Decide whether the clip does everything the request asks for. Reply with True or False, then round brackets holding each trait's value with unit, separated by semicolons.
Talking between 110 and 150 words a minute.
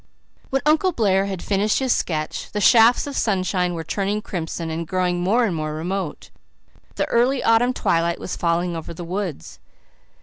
False (170 wpm)